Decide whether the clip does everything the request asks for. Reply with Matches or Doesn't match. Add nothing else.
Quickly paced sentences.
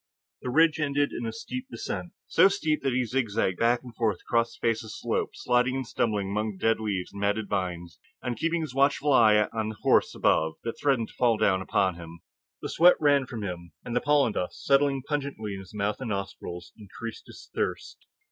Matches